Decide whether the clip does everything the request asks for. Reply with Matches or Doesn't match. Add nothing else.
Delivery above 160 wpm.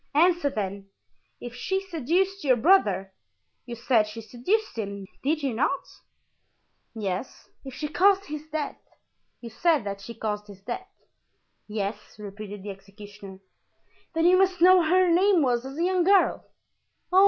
Doesn't match